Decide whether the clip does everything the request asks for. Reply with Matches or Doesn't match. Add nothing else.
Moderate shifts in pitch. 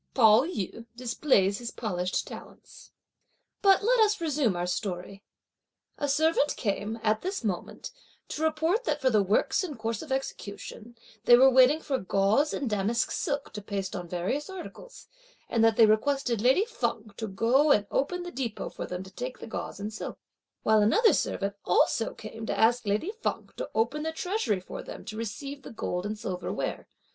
Doesn't match